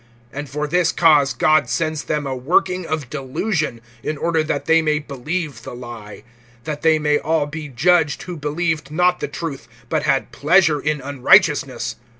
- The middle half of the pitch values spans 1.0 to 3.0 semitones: Yes, average, 2.7 semitones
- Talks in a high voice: No, medium, 150 Hz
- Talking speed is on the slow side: No, average, 170 wpm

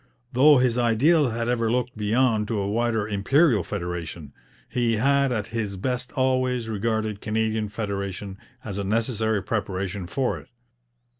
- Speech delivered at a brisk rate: No, average, 145 wpm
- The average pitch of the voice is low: Yes, low, 110 Hz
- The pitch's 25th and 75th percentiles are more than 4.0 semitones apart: No, average, 3.5 semitones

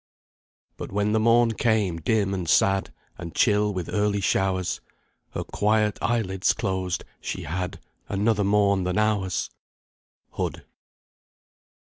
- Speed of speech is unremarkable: No, slow, 120 wpm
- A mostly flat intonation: Yes, narrow, 2.3 semitones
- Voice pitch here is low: Yes, low, 100 Hz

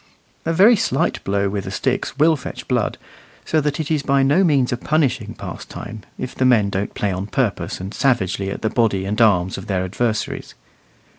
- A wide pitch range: Yes, wide, 6.2 semitones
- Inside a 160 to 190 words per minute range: No, average, 200 wpm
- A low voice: Yes, low, 120 Hz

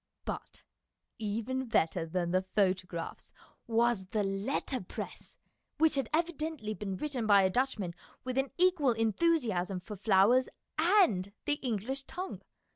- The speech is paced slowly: Yes, slow, 125 wpm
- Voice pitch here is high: Yes, high, 225 Hz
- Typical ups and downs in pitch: No, wide, 6.1 semitones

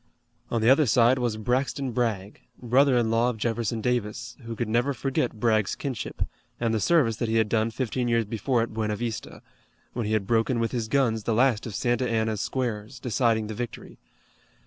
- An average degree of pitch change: No, narrow, 2.0 semitones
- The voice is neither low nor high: No, low, 115 Hz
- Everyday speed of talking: Yes, average, 195 wpm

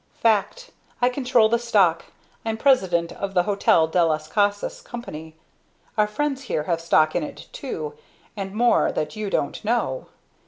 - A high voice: Yes, high, 205 Hz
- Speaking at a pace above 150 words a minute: Yes, average, 160 wpm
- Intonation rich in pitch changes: Yes, wide, 6.2 semitones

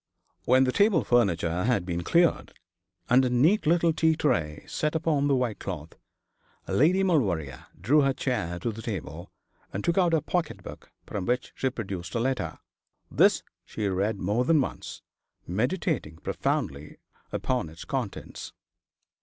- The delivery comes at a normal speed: Yes, average, 155 wpm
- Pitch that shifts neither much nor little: No, wide, 8.9 semitones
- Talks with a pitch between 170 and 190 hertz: No, low, 125 Hz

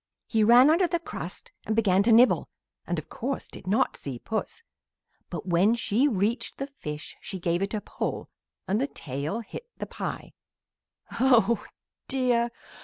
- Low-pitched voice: No, high, 225 Hz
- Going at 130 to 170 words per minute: Yes, average, 165 wpm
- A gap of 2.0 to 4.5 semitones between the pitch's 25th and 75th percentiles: No, average, 4.9 semitones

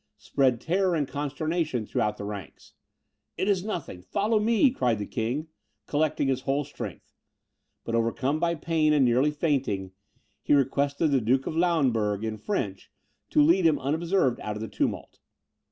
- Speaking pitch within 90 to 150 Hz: Yes, medium, 140 Hz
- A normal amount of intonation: No, wide, 6.0 semitones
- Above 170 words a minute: No, average, 165 wpm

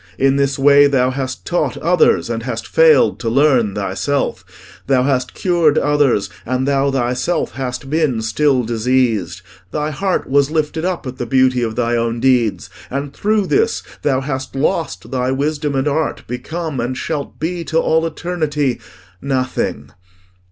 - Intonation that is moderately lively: Yes, average, 3.4 semitones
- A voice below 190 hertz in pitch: Yes, low, 135 Hz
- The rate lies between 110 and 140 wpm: No, average, 160 wpm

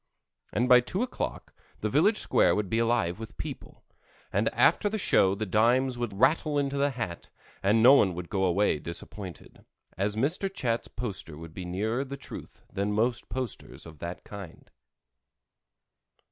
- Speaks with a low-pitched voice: Yes, low, 110 Hz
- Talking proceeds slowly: No, average, 165 wpm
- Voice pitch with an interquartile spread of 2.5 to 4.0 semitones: No, wide, 5.4 semitones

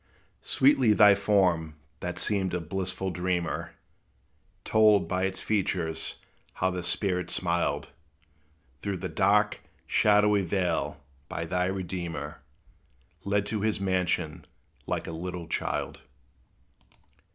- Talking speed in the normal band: No, slow, 110 wpm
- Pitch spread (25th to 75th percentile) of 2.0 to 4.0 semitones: Yes, narrow, 2.5 semitones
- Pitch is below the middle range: Yes, very low, 95 Hz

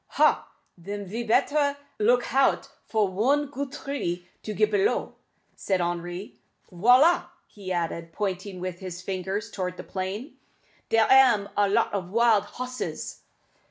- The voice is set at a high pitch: Yes, high, 205 Hz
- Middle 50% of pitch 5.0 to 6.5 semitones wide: Yes, wide, 5.4 semitones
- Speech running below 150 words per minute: Yes, average, 140 wpm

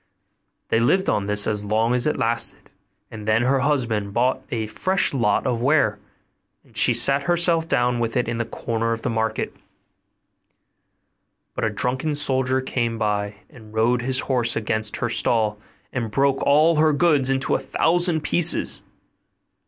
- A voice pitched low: Yes, low, 120 Hz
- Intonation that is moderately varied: Yes, average, 3.8 semitones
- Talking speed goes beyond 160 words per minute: Yes, average, 170 wpm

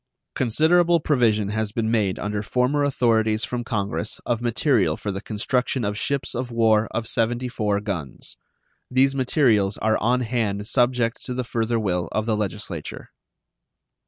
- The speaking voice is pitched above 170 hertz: No, low, 115 Hz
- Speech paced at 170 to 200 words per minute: No, average, 150 wpm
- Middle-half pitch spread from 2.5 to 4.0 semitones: Yes, average, 3.0 semitones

